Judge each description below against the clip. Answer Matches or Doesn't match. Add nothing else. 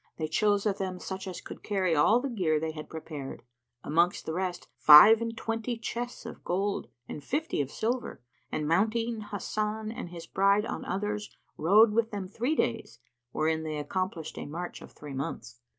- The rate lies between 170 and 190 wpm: Matches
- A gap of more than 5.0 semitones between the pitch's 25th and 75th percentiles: Matches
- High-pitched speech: Matches